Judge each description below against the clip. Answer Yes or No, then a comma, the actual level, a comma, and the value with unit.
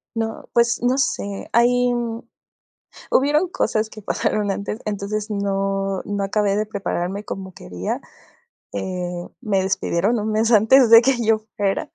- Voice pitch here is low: No, high, 210 Hz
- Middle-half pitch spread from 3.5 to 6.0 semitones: No, average, 2.8 semitones